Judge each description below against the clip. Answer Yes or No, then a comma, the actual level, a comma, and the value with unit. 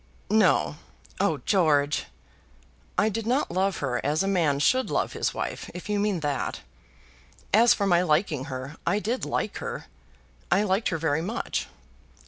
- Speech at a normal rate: Yes, average, 160 wpm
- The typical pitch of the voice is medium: Yes, medium, 180 Hz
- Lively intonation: Yes, wide, 5.7 semitones